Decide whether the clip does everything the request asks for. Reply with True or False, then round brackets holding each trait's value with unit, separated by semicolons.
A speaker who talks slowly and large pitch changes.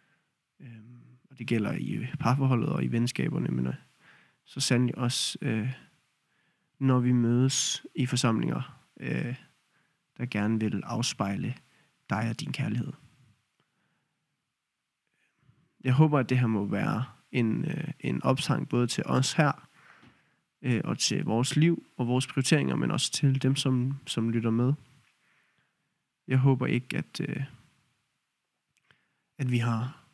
False (120 wpm; 2.9 semitones)